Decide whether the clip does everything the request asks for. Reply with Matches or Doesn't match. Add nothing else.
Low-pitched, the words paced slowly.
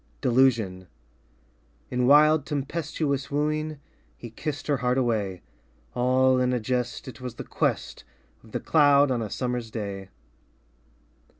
Matches